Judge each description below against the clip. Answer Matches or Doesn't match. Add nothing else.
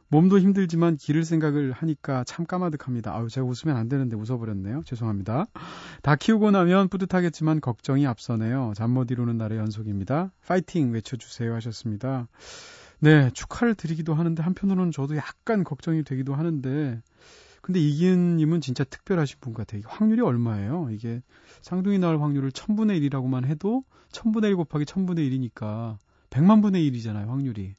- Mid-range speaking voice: Matches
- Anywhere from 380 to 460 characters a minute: Matches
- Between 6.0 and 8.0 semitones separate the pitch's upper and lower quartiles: Matches